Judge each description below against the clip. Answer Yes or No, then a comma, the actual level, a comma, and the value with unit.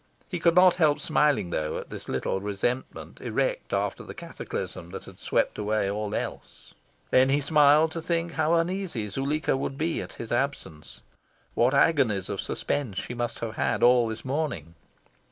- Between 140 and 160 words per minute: No, average, 170 wpm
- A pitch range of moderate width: No, wide, 6.7 semitones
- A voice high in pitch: No, low, 135 Hz